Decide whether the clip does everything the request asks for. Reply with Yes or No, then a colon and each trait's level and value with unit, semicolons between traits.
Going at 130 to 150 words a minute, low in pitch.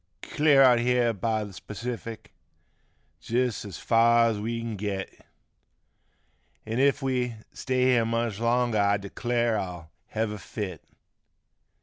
Yes: slow, 135 wpm; low, 115 Hz